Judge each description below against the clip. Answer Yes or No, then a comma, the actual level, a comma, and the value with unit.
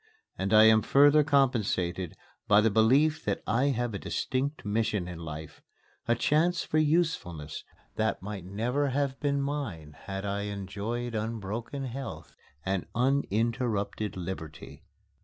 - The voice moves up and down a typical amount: No, wide, 5.9 semitones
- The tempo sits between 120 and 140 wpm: Yes, slow, 135 wpm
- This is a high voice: No, low, 110 Hz